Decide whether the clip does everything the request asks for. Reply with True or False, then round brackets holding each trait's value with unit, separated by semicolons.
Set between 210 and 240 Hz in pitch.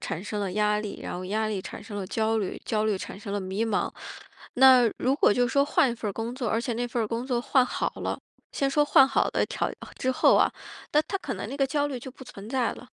True (235 Hz)